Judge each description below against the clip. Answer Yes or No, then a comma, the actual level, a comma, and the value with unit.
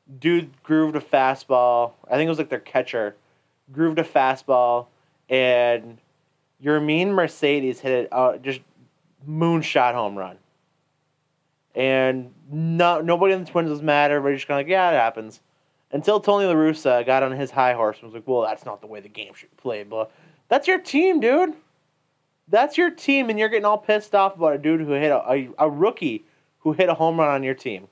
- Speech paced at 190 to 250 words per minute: Yes, average, 200 wpm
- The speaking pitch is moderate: Yes, medium, 150 Hz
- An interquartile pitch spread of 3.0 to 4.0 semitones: No, average, 4.9 semitones